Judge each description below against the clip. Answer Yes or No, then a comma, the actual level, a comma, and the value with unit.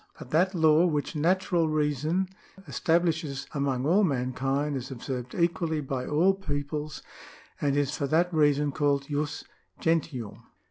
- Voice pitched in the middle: Yes, medium, 150 Hz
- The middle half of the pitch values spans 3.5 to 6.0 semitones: No, average, 2.9 semitones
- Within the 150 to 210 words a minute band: No, slow, 135 wpm